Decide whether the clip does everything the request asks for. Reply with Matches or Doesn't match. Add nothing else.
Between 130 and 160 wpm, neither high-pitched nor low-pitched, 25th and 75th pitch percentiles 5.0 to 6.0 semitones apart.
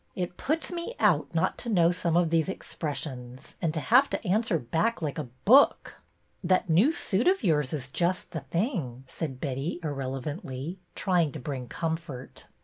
Doesn't match